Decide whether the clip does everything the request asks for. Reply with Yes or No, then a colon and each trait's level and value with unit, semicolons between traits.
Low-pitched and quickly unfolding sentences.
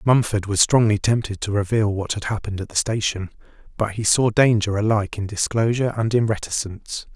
No: low, 105 Hz; average, 185 wpm